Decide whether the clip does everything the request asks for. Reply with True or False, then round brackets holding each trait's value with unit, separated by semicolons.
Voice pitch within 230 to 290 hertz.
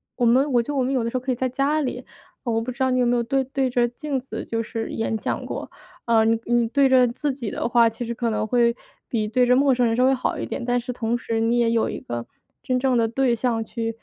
True (240 Hz)